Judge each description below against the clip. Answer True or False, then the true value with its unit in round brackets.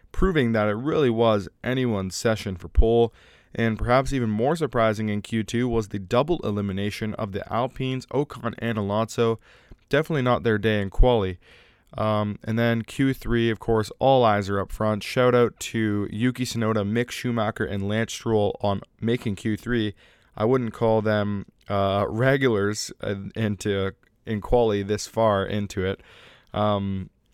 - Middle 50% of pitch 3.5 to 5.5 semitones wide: False (2.5 semitones)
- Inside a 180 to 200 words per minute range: False (155 wpm)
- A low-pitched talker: True (110 Hz)